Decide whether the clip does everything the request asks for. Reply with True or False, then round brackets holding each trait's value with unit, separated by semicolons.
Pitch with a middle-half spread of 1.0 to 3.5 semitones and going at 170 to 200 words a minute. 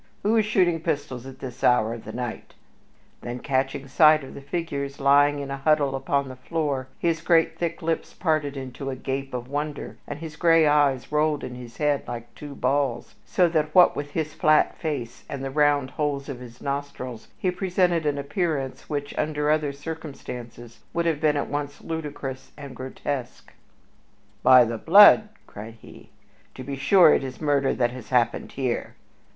True (2.9 semitones; 180 wpm)